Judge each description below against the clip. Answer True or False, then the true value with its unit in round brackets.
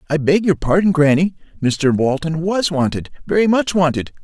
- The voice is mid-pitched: True (165 Hz)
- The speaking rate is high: False (155 wpm)